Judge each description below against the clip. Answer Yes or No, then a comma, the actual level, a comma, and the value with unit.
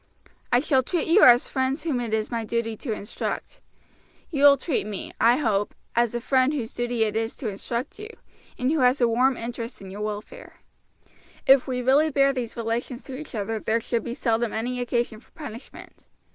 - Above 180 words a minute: Yes, average, 200 wpm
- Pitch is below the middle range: No, high, 240 Hz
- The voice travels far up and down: No, average, 3.0 semitones